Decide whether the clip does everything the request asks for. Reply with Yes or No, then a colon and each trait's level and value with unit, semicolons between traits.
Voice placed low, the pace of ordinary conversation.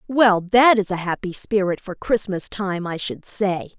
No: high, 200 Hz; average, 190 wpm